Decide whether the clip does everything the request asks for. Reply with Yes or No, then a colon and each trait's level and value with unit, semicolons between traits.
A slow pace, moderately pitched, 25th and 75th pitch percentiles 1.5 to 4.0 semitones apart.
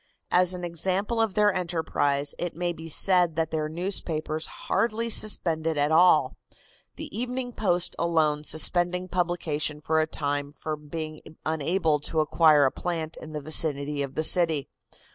No: average, 155 wpm; medium, 160 Hz; average, 2.8 semitones